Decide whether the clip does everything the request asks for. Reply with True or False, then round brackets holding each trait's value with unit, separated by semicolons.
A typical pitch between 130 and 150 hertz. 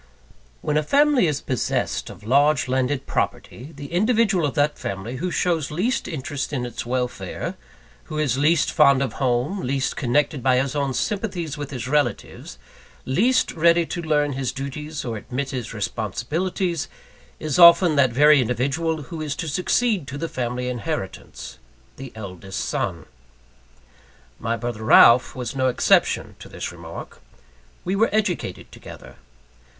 True (140 Hz)